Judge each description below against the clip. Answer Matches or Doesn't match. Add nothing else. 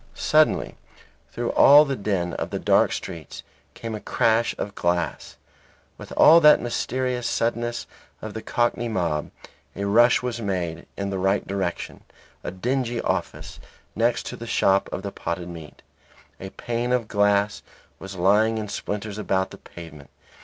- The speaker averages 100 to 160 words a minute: Matches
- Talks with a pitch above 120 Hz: Doesn't match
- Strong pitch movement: Doesn't match